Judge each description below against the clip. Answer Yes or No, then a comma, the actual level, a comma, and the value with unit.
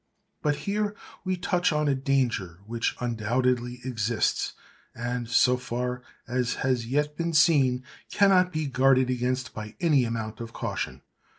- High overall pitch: No, low, 125 Hz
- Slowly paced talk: Yes, slow, 130 wpm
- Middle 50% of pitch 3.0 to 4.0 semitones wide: Yes, average, 3.7 semitones